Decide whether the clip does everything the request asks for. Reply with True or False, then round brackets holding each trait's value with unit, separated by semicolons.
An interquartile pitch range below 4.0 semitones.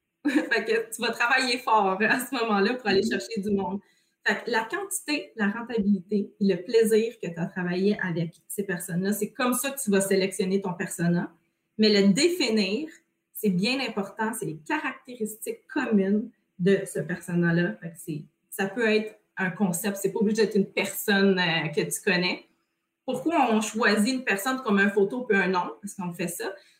True (2.9 semitones)